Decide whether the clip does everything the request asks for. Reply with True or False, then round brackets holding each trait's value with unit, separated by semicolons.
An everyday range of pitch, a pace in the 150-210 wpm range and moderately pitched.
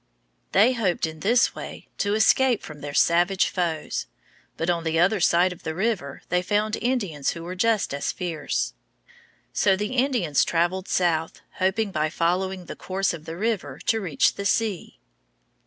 True (4.1 semitones; 170 wpm; 180 Hz)